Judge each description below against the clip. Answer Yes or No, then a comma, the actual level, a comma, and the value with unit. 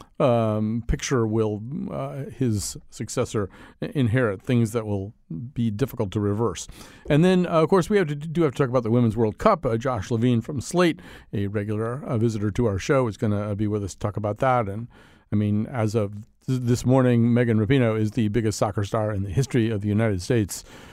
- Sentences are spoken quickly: Yes, fast, 215 wpm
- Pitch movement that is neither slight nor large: Yes, average, 3.4 semitones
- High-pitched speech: No, low, 115 Hz